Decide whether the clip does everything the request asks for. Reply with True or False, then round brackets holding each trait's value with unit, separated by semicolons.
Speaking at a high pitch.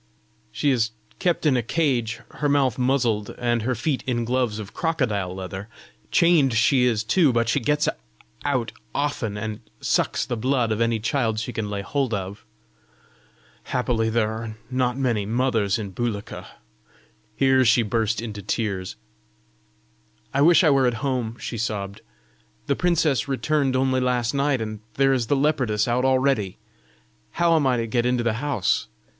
False (120 Hz)